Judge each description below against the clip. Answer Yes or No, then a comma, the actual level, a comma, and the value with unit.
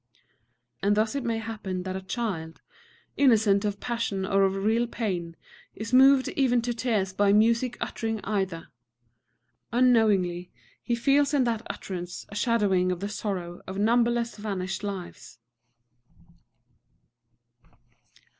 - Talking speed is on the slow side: Yes, slow, 125 wpm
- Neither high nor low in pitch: No, high, 210 Hz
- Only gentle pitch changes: No, average, 3.7 semitones